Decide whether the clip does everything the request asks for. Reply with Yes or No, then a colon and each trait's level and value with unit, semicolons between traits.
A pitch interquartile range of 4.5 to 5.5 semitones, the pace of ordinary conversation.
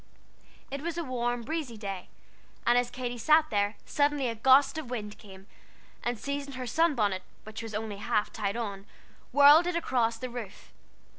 Yes: average, 4.8 semitones; average, 175 wpm